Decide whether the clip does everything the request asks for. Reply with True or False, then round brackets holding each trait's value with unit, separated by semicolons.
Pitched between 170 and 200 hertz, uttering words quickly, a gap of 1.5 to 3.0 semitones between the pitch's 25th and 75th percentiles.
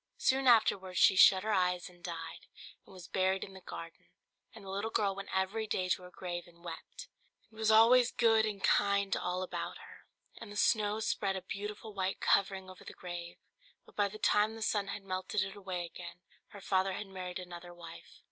True (190 Hz; 210 wpm; 2.5 semitones)